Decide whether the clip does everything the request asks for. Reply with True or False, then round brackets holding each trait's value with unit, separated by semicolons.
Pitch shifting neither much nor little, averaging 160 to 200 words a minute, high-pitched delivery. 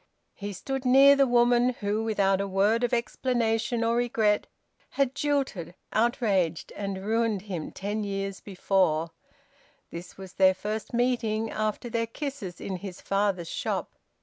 False (3.7 semitones; 145 wpm; 215 Hz)